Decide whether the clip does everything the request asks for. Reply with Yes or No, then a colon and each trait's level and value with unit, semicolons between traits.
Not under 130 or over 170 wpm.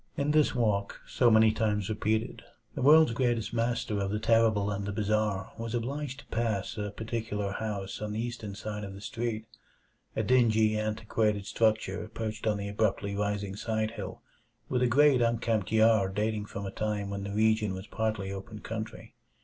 No: average, 180 wpm